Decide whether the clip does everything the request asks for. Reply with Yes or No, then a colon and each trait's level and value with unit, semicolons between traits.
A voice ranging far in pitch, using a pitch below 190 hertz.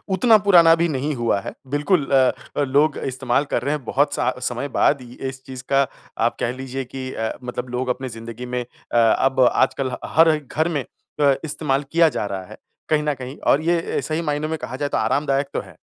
No: average, 3.2 semitones; low, 135 Hz